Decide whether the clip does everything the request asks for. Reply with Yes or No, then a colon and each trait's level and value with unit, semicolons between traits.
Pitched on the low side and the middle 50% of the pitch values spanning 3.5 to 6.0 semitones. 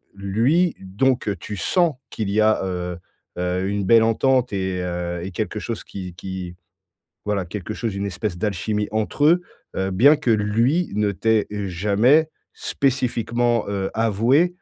Yes: low, 105 Hz; average, 4.0 semitones